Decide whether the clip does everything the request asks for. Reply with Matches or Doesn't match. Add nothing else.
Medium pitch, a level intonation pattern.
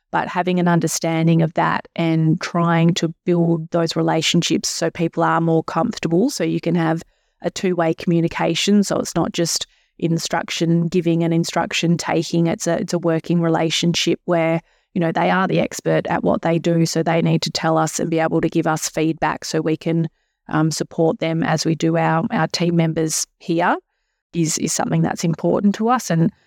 Matches